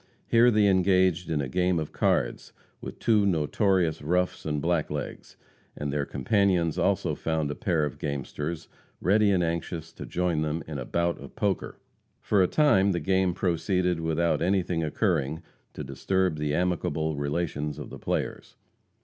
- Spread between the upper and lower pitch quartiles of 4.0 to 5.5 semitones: No, average, 3.5 semitones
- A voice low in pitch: Yes, very low, 85 Hz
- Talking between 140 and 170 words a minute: Yes, average, 160 wpm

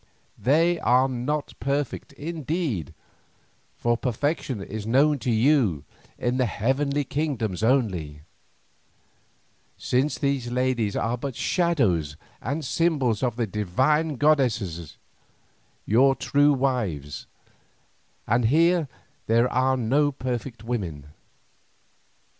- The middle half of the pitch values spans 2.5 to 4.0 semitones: No, average, 4.7 semitones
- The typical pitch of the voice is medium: No, low, 125 Hz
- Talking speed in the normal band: No, slow, 100 wpm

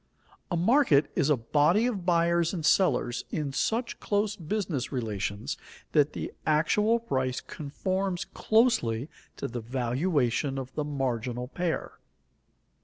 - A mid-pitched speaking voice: Yes, medium, 150 Hz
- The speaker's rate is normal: No, slow, 125 wpm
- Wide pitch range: Yes, wide, 6.5 semitones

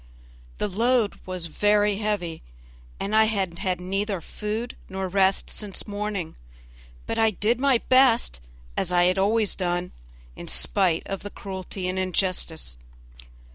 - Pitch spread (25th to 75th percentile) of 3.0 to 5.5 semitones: No, narrow, 2.6 semitones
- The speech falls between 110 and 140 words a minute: Yes, slow, 135 wpm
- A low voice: No, high, 195 Hz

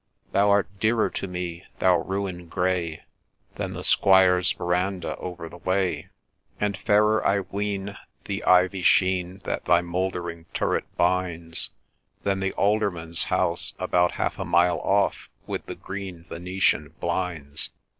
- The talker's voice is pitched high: No, very low, 90 Hz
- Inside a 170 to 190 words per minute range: No, slow, 135 wpm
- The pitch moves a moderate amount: No, narrow, 2.0 semitones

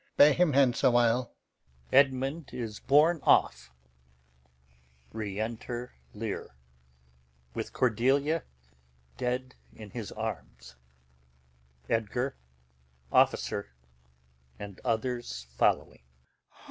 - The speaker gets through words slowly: Yes, slow, 75 wpm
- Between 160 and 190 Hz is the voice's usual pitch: No, low, 120 Hz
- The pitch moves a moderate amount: Yes, average, 3.6 semitones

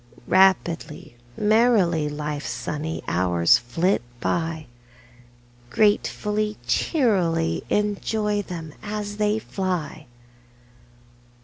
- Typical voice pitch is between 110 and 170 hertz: No, medium, 180 Hz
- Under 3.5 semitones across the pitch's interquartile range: No, average, 5.3 semitones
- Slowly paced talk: Yes, slow, 75 wpm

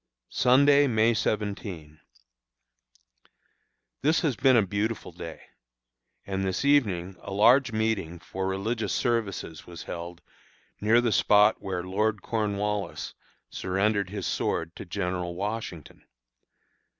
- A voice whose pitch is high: No, low, 105 Hz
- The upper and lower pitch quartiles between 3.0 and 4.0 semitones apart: Yes, average, 3.6 semitones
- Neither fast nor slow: No, slow, 115 wpm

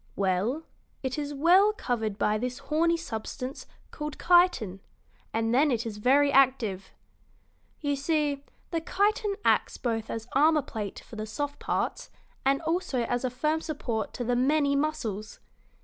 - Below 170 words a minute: Yes, average, 150 wpm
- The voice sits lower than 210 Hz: No, very high, 270 Hz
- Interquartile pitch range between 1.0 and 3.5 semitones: No, wide, 5.4 semitones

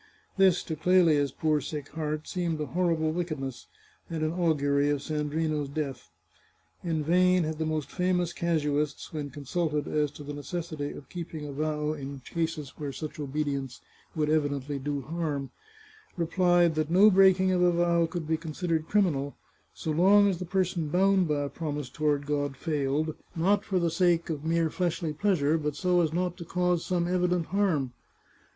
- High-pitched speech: No, medium, 160 Hz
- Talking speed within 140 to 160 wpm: No, average, 175 wpm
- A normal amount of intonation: Yes, average, 3.1 semitones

